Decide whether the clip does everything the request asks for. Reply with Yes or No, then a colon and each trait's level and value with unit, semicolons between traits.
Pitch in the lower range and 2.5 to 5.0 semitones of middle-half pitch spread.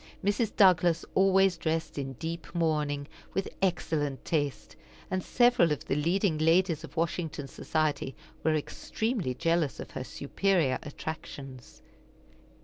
No: medium, 160 Hz; average, 4.1 semitones